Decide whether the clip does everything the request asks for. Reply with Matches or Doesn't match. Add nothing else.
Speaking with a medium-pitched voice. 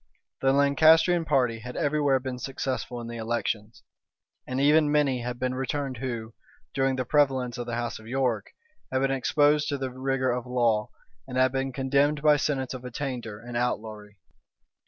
Doesn't match